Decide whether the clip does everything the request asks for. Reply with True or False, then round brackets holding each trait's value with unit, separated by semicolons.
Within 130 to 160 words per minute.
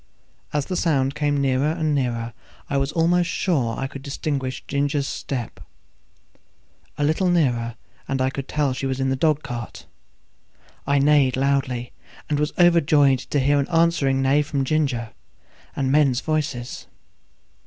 True (155 wpm)